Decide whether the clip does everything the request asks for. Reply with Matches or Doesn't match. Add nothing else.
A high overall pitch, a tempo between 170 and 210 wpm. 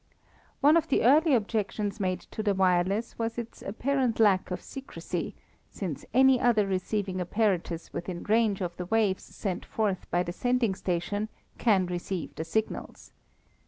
Doesn't match